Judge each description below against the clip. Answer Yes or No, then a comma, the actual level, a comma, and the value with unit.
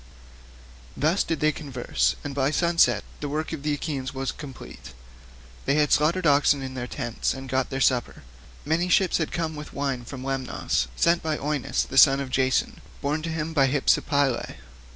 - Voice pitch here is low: No, medium, 145 Hz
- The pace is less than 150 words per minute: No, average, 180 wpm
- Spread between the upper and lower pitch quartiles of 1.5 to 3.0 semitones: Yes, average, 2.7 semitones